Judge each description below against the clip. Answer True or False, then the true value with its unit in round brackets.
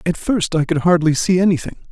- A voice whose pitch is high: False (170 Hz)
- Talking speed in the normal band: False (220 wpm)